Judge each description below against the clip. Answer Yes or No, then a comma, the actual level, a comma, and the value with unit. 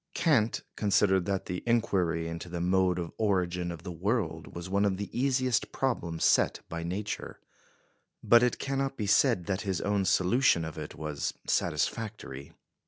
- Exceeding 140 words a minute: Yes, average, 165 wpm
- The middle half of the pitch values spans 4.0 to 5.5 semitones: Yes, average, 4.6 semitones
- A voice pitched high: No, very low, 95 Hz